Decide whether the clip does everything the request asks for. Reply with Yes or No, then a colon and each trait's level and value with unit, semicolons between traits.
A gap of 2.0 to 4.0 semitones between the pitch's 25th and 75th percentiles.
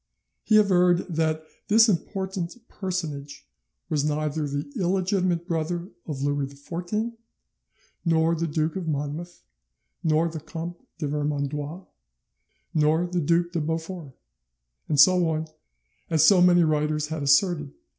Yes: average, 2.9 semitones